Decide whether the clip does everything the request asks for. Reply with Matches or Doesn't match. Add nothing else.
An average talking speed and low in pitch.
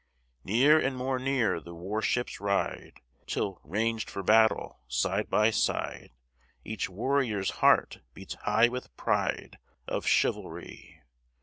Doesn't match